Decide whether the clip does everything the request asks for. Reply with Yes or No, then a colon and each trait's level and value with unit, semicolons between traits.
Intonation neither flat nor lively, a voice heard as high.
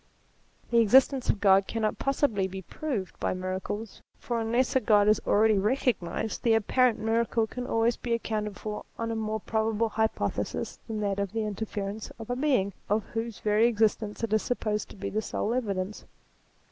No: narrow, 2.1 semitones; high, 220 Hz